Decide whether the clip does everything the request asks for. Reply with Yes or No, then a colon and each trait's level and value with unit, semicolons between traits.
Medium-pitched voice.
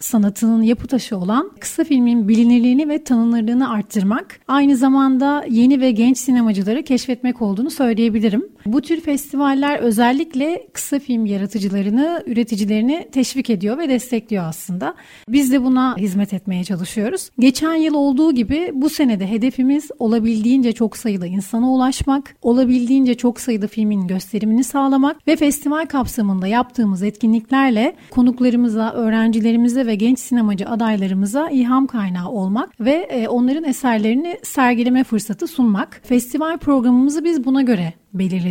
No: high, 245 Hz